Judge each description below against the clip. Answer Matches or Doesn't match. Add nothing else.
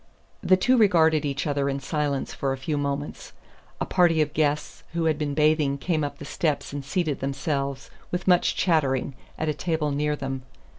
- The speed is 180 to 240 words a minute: Matches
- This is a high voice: Doesn't match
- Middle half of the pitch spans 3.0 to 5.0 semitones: Doesn't match